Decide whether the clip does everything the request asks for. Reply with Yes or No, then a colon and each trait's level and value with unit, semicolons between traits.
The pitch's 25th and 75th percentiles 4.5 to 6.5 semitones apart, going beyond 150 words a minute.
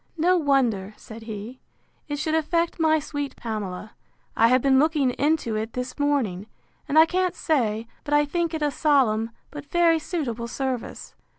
Yes: wide, 5.6 semitones; average, 170 wpm